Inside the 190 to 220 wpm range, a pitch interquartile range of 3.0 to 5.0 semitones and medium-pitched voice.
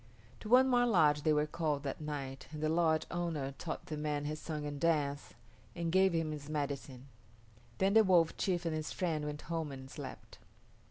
No: average, 200 wpm; narrow, 2.5 semitones; medium, 155 Hz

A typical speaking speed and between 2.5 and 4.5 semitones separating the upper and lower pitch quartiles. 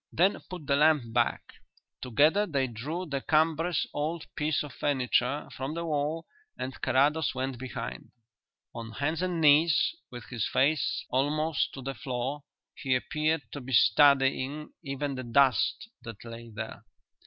Yes: average, 150 wpm; average, 3.3 semitones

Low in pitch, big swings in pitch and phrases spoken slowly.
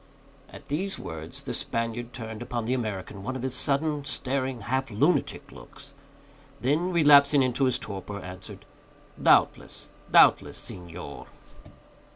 No: low, 125 Hz; average, 5.0 semitones; slow, 130 wpm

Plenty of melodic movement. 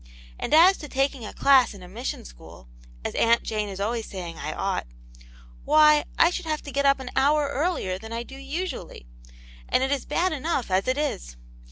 Yes: wide, 5.9 semitones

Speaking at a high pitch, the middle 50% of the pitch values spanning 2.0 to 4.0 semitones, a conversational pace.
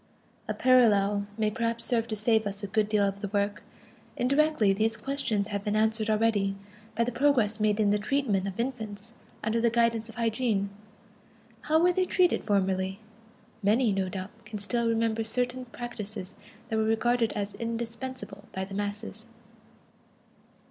Yes: high, 220 Hz; narrow, 2.6 semitones; average, 160 wpm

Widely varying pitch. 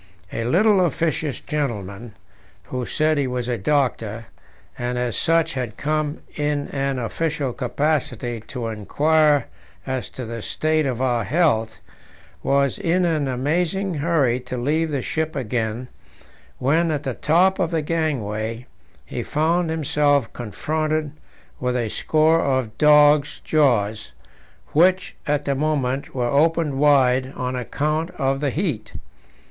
No: average, 4.1 semitones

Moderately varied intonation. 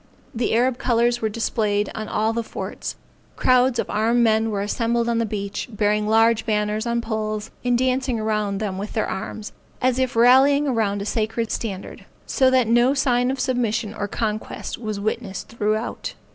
No: narrow, 2.3 semitones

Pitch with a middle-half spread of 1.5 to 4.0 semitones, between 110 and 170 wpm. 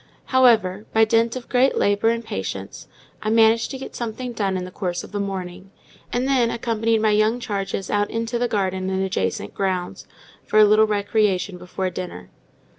No: average, 3.4 semitones; average, 185 wpm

